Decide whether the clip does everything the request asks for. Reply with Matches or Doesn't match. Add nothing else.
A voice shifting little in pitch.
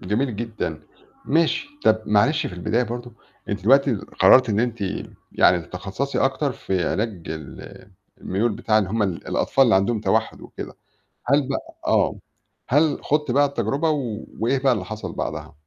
Doesn't match